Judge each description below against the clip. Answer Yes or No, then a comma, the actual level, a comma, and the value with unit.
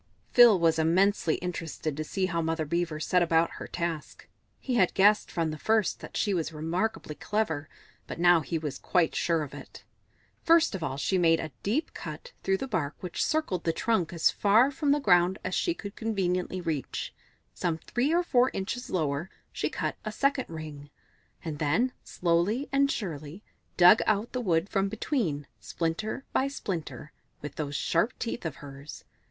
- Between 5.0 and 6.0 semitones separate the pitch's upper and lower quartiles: Yes, average, 5.3 semitones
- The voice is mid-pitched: Yes, medium, 175 Hz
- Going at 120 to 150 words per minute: No, average, 180 wpm